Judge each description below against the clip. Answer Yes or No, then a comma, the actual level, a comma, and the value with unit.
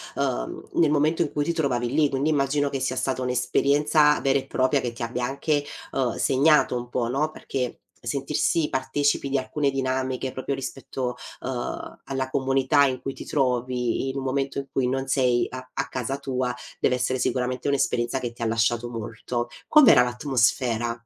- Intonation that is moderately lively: No, narrow, 2.0 semitones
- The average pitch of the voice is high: No, low, 130 Hz